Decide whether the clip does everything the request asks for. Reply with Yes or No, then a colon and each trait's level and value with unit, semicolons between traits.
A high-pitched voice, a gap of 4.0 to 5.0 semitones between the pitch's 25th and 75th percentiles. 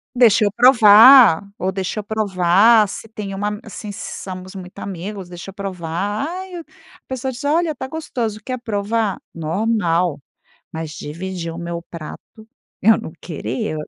Yes: high, 205 Hz; average, 4.4 semitones